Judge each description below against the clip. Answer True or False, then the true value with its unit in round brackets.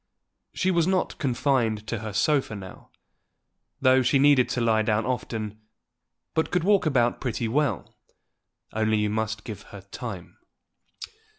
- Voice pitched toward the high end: False (115 Hz)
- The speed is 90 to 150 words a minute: True (140 wpm)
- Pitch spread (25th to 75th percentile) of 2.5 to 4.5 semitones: True (4.2 semitones)